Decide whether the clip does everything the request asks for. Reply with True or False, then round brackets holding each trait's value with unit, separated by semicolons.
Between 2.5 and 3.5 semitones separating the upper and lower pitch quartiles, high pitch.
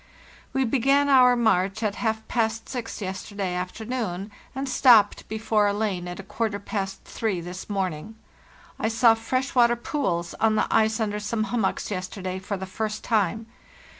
True (3.1 semitones; 215 Hz)